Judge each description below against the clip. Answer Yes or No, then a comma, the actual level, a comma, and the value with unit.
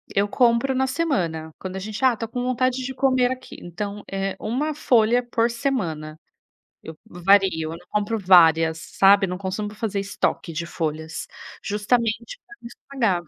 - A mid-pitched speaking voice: No, high, 210 Hz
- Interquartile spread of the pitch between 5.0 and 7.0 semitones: Yes, wide, 5.5 semitones